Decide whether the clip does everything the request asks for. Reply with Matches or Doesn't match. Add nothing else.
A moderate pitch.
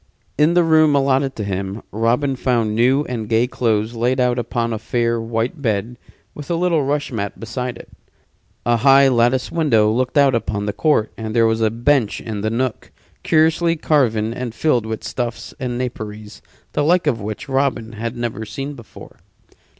Doesn't match